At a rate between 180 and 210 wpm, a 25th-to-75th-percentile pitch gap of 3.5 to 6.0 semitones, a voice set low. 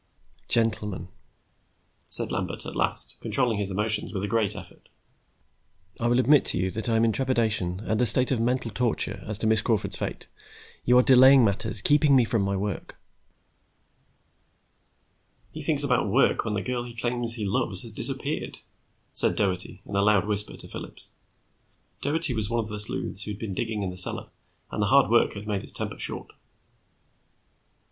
No: average, 185 wpm; average, 3.0 semitones; low, 110 Hz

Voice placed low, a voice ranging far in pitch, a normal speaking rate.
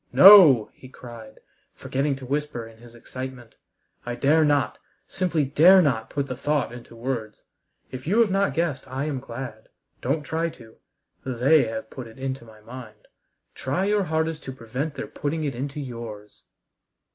No: low, 130 Hz; average, 4.4 semitones; average, 170 wpm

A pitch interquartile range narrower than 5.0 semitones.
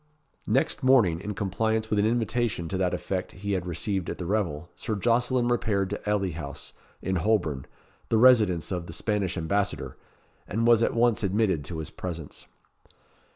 Yes: average, 4.0 semitones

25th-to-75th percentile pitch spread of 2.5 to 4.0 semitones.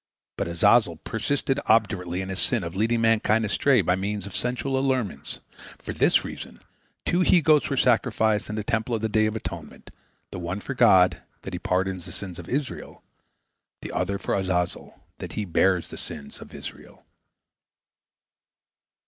No: average, 4.5 semitones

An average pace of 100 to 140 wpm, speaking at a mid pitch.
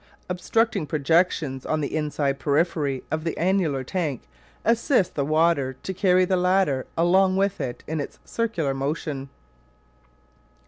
Yes: slow, 135 wpm; medium, 160 Hz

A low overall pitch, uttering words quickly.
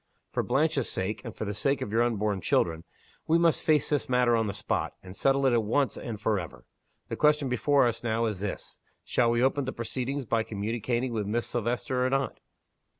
Yes: low, 120 Hz; fast, 210 wpm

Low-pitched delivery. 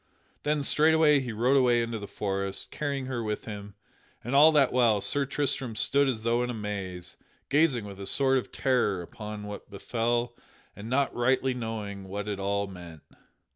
Yes: low, 115 Hz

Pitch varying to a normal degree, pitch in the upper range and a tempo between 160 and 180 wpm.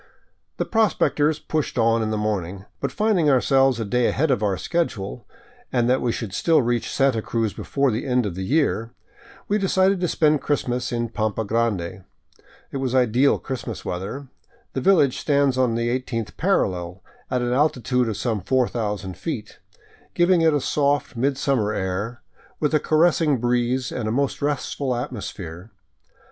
No: average, 4.5 semitones; low, 125 Hz; average, 165 wpm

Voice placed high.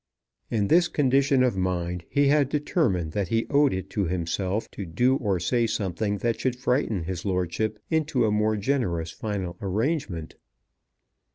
No: low, 105 Hz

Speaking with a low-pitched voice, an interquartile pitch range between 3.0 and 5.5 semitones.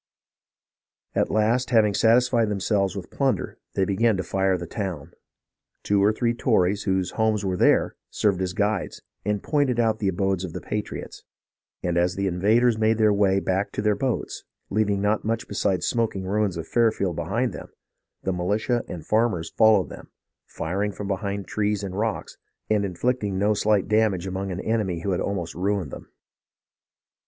No: low, 100 Hz; narrow, 2.5 semitones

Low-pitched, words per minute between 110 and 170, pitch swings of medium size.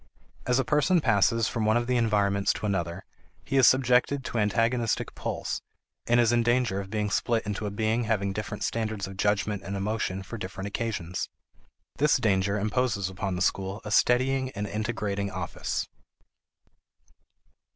Yes: low, 105 Hz; average, 160 wpm; average, 3.2 semitones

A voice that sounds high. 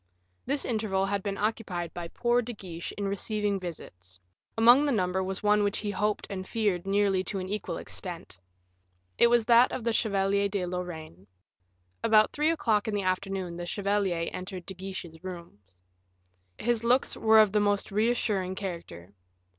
Yes: high, 200 Hz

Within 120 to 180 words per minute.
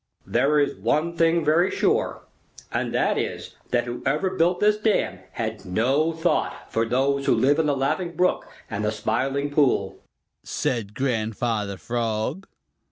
Yes: average, 150 wpm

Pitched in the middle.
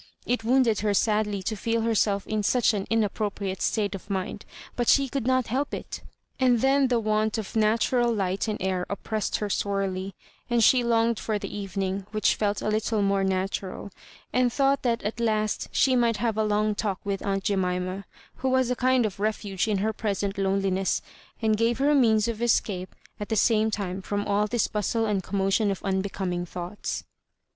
No: high, 210 Hz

